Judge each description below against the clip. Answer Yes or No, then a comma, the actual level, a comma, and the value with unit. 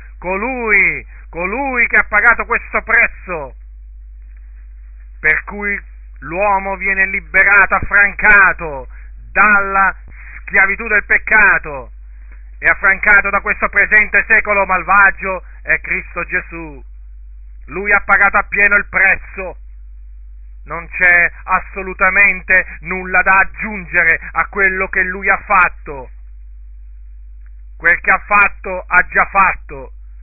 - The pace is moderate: No, slow, 105 wpm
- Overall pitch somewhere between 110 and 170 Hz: No, medium, 185 Hz